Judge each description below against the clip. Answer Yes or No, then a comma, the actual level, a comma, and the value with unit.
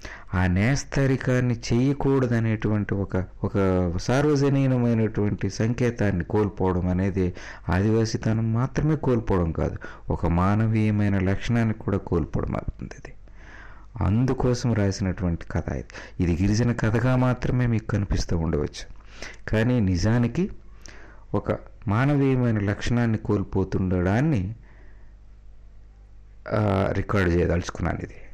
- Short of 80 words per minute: No, average, 85 wpm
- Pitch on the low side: Yes, low, 105 Hz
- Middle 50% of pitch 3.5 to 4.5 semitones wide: Yes, average, 3.9 semitones